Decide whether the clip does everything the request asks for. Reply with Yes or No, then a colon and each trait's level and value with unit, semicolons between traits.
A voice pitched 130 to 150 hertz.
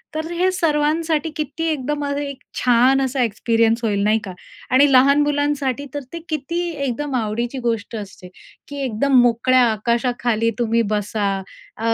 No: very high, 260 Hz